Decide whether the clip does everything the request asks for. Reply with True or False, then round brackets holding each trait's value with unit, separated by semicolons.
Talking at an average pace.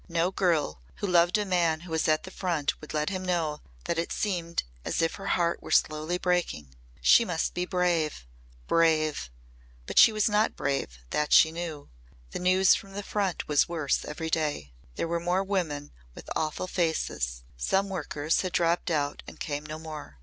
True (185 wpm)